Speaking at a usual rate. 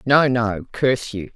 Yes: average, 180 wpm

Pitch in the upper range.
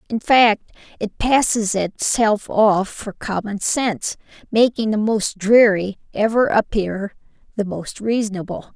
Yes: high, 210 Hz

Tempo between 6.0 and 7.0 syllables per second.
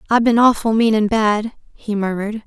No: 5.4 syllables/s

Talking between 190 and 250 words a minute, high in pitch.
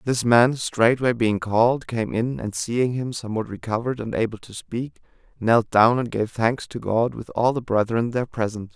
No: average, 200 wpm; low, 115 Hz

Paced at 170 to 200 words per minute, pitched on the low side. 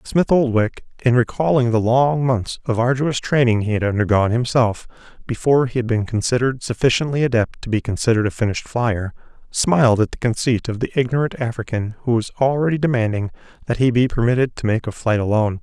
Yes: average, 185 wpm; low, 120 Hz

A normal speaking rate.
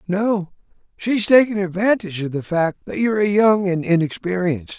Yes: average, 165 wpm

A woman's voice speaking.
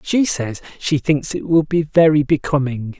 No: male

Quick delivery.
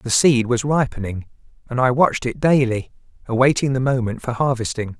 No: average, 170 wpm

